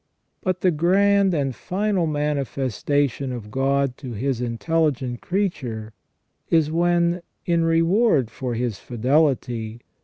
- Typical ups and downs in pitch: No, wide, 5.7 semitones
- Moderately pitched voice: Yes, medium, 145 Hz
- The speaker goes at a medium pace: No, slow, 120 wpm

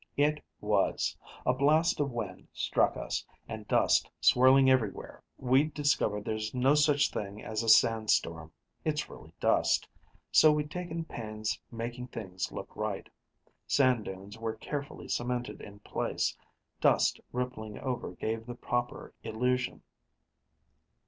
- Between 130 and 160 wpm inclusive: Yes, slow, 135 wpm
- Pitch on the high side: No, low, 120 Hz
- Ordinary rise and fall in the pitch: Yes, average, 4.3 semitones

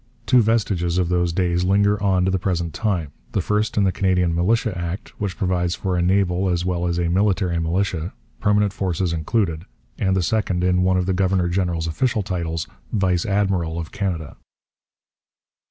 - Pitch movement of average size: No, narrow, 2.2 semitones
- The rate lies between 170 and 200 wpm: Yes, average, 180 wpm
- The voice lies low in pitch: Yes, very low, 90 Hz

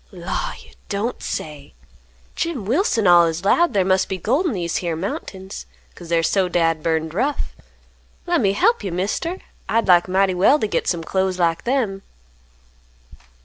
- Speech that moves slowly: No, average, 160 wpm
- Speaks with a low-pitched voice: No, high, 190 Hz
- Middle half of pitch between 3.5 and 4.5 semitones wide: No, average, 5.0 semitones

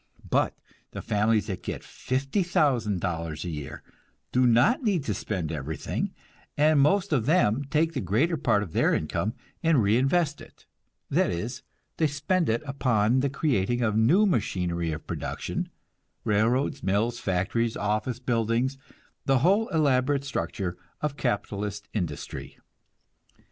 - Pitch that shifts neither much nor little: No, wide, 5.9 semitones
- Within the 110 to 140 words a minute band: Yes, slow, 135 wpm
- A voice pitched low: Yes, low, 120 Hz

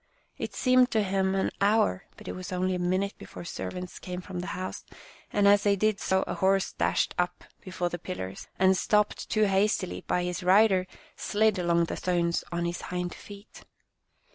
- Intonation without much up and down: Yes, narrow, 2.1 semitones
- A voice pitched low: No, medium, 185 Hz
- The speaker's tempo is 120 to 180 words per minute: No, average, 190 wpm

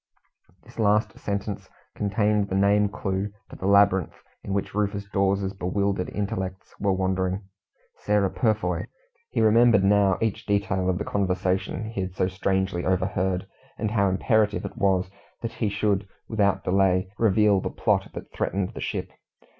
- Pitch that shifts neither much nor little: No, narrow, 1.6 semitones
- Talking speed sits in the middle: Yes, average, 155 wpm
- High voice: No, low, 100 Hz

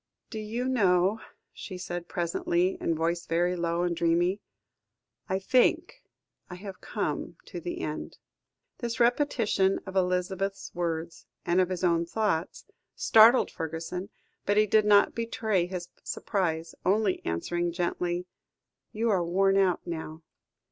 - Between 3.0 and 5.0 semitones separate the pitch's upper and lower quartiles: Yes, average, 3.4 semitones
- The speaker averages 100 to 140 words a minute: Yes, slow, 135 wpm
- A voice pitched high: No, medium, 180 Hz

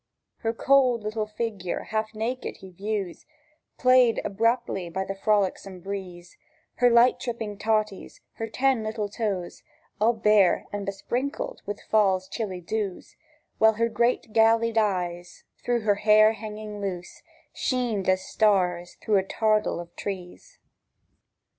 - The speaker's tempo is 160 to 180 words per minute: No, slow, 135 wpm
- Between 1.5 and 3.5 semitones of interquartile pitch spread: Yes, average, 2.8 semitones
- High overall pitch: Yes, high, 215 Hz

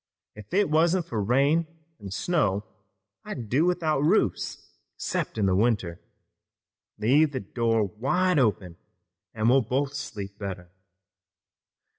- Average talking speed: No, slow, 120 wpm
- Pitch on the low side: Yes, low, 120 Hz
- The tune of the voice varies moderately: No, wide, 6.9 semitones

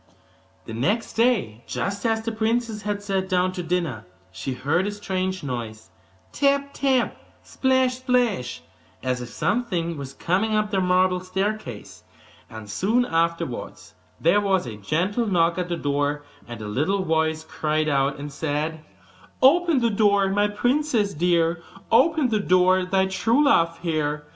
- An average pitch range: No, wide, 6.1 semitones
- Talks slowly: No, average, 155 wpm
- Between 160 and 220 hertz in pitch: Yes, medium, 185 Hz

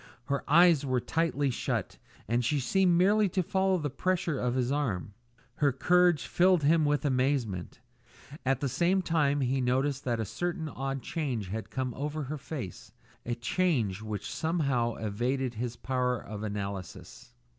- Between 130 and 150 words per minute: No, average, 160 wpm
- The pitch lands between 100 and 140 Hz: Yes, low, 135 Hz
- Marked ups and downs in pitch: No, average, 5.0 semitones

